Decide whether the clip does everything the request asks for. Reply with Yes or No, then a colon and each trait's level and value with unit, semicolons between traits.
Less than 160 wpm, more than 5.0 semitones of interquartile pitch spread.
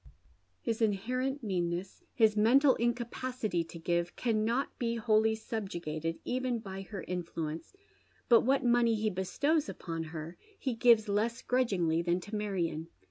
Yes: average, 140 wpm; wide, 5.4 semitones